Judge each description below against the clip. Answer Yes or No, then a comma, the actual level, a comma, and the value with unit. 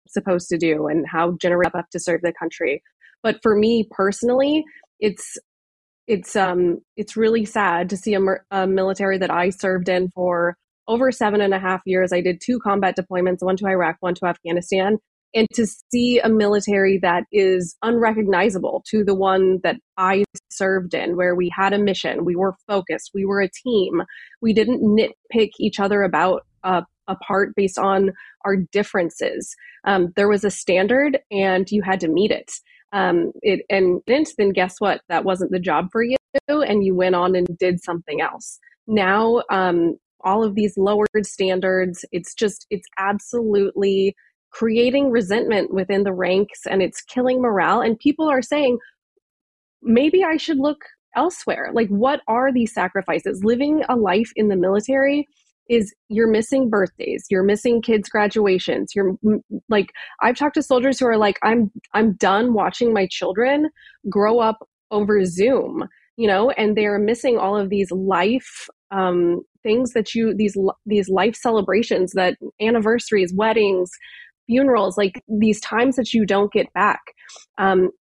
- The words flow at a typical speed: Yes, average, 165 wpm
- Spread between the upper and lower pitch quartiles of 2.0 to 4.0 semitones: Yes, average, 3.4 semitones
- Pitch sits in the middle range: No, high, 205 Hz